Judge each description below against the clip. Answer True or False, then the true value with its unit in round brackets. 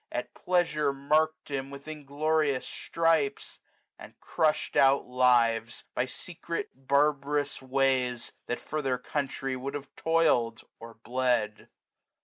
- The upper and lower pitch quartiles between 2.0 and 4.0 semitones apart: True (3.2 semitones)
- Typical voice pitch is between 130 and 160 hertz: True (140 Hz)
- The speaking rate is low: True (120 wpm)